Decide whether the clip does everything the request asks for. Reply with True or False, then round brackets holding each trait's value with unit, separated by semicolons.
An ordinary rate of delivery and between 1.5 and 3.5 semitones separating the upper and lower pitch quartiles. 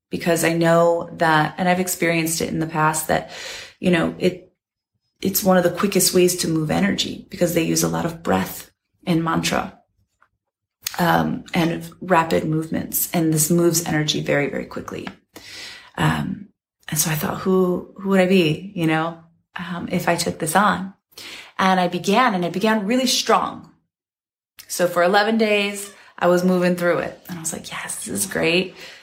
True (180 wpm; 2.5 semitones)